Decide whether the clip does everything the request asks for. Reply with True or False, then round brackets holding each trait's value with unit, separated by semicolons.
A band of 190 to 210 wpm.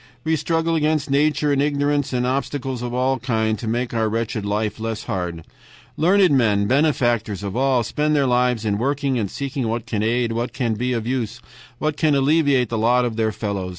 True (195 wpm)